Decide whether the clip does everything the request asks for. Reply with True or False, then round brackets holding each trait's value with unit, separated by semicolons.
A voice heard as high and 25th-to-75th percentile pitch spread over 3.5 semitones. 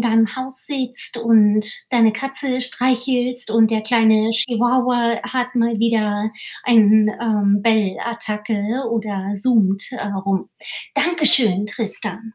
False (225 Hz; 2.6 semitones)